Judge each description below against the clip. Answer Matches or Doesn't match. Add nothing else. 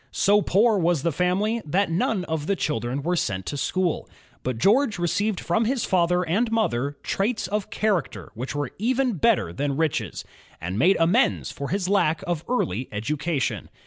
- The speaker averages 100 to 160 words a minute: Doesn't match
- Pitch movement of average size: Doesn't match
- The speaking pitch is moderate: Matches